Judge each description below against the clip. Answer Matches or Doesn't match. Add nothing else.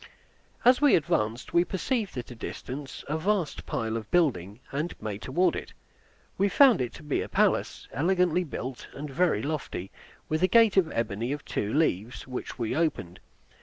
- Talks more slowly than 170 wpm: Doesn't match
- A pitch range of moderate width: Doesn't match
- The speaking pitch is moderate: Matches